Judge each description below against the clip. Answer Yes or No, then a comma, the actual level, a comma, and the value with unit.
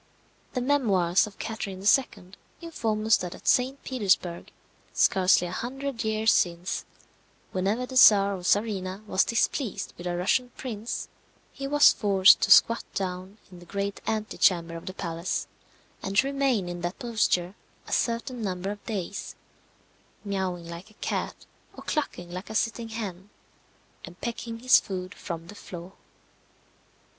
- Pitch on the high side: Yes, high, 200 Hz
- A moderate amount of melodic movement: Yes, average, 4.1 semitones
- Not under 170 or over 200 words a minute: No, average, 150 wpm